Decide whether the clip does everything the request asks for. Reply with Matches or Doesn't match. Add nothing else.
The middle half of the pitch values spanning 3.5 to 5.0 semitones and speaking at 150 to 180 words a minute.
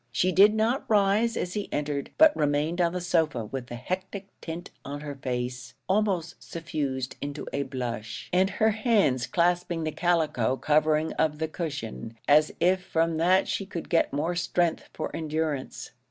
Matches